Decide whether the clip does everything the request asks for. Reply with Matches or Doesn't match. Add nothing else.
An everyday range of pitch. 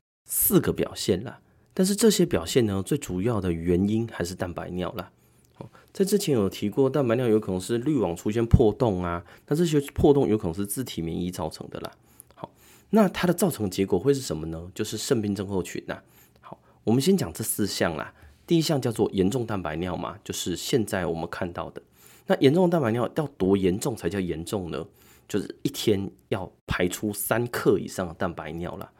Doesn't match